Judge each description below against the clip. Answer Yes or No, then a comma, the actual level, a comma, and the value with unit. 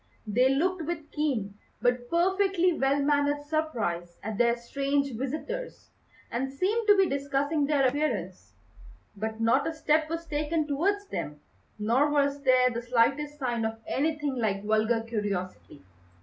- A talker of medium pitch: No, very high, 275 Hz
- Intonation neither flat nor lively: Yes, average, 4.9 semitones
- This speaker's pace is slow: No, average, 145 wpm